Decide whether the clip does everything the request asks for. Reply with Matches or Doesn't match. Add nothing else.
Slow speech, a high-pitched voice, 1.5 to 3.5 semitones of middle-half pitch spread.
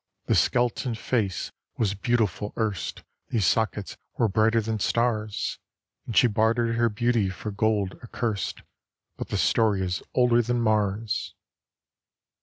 Doesn't match